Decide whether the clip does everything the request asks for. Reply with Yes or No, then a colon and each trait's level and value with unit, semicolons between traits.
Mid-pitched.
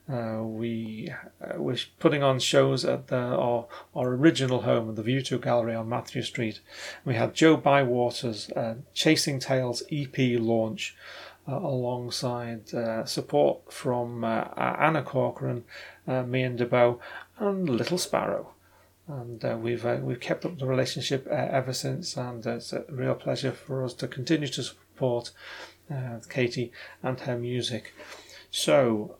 No: low, 125 Hz